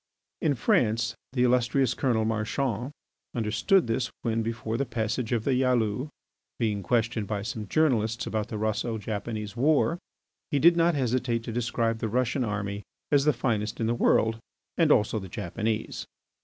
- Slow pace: No, average, 160 wpm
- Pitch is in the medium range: No, low, 115 Hz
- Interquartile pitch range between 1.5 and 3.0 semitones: Yes, average, 2.7 semitones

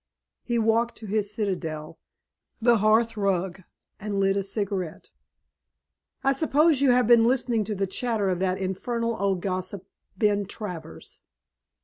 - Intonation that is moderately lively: Yes, average, 3.4 semitones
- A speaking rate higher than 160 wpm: No, average, 140 wpm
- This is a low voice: No, high, 205 Hz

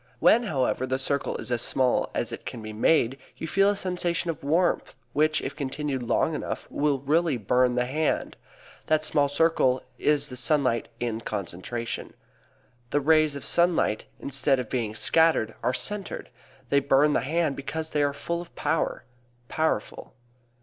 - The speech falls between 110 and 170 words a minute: Yes, average, 165 wpm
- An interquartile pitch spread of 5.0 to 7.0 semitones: No, average, 4.0 semitones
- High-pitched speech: No, medium, 140 Hz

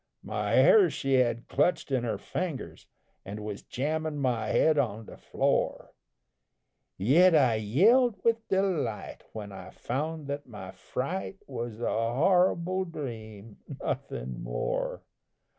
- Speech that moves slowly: Yes, slow, 125 wpm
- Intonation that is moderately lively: No, wide, 7.5 semitones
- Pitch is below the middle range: Yes, low, 130 Hz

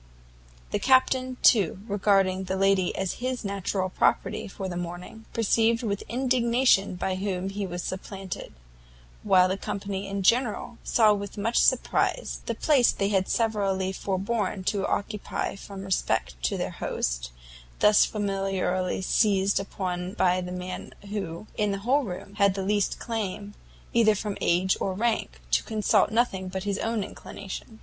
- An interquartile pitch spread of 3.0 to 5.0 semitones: No, narrow, 2.6 semitones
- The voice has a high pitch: Yes, high, 195 Hz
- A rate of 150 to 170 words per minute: Yes, average, 155 wpm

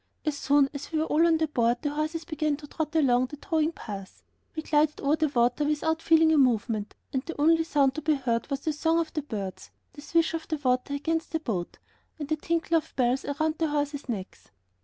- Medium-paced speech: No, fast, 230 wpm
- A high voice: Yes, very high, 295 Hz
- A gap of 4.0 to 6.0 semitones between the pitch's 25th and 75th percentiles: No, average, 3.2 semitones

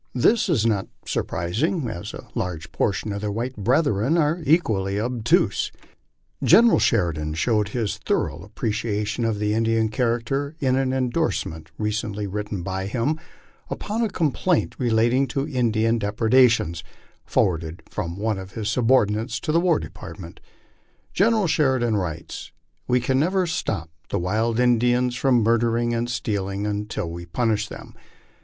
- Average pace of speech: Yes, average, 150 wpm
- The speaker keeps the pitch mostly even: No, average, 4.2 semitones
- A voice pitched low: Yes, low, 115 Hz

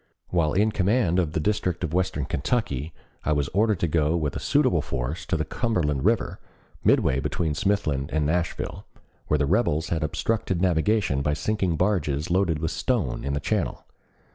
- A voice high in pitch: No, very low, 80 Hz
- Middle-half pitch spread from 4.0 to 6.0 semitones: Yes, average, 4.5 semitones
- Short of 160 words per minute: No, average, 175 wpm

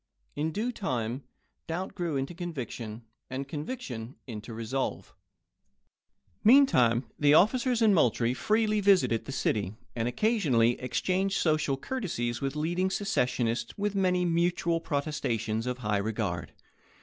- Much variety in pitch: Yes, wide, 7.9 semitones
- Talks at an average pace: No, slow, 125 wpm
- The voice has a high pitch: No, medium, 145 Hz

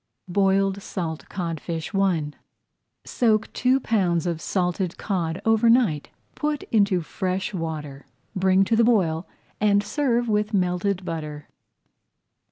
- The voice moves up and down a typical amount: Yes, average, 4.0 semitones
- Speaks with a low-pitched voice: No, high, 190 Hz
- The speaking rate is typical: No, slow, 120 wpm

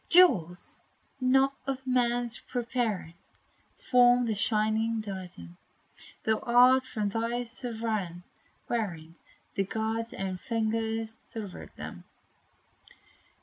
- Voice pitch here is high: Yes, high, 225 Hz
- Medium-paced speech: No, slow, 90 wpm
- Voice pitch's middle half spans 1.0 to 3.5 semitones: Yes, average, 2.7 semitones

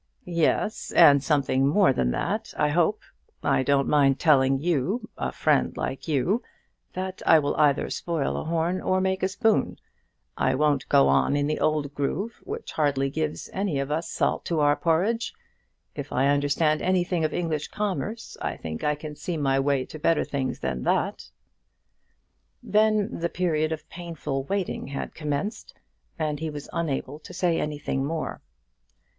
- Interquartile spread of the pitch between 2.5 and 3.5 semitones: No, average, 3.9 semitones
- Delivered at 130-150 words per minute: No, average, 165 wpm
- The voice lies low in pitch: No, medium, 155 Hz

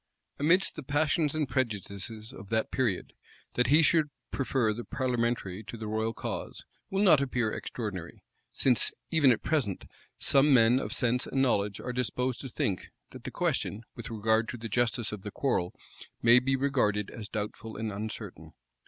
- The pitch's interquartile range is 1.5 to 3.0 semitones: No, average, 3.9 semitones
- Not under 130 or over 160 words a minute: No, average, 175 wpm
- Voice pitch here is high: No, low, 120 Hz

